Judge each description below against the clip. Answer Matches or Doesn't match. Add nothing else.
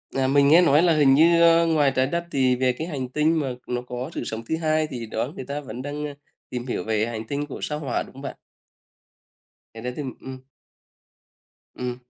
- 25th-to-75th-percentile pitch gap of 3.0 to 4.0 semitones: Matches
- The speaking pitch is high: Doesn't match